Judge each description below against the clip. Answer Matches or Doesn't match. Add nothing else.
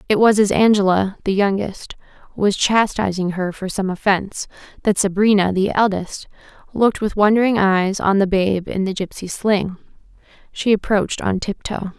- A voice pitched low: Doesn't match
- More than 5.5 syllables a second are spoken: Doesn't match